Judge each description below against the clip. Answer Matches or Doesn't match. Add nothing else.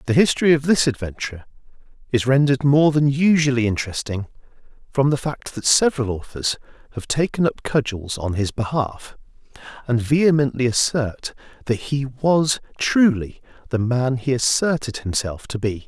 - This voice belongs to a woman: Doesn't match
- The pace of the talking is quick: Doesn't match